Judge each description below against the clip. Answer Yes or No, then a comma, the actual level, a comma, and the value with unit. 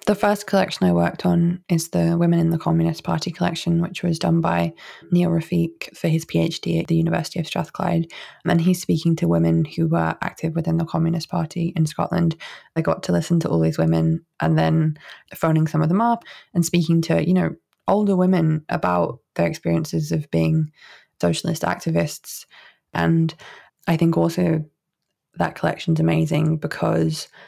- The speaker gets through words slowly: No, average, 175 wpm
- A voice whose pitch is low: No, medium, 165 Hz